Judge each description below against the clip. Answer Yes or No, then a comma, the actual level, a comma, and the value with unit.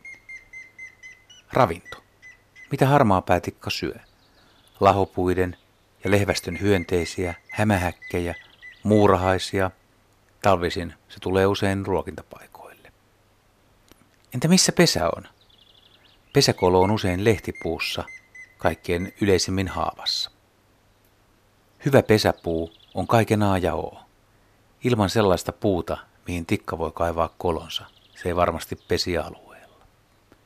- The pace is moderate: No, slow, 90 wpm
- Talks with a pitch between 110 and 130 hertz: No, low, 100 Hz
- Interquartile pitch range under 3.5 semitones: Yes, average, 2.9 semitones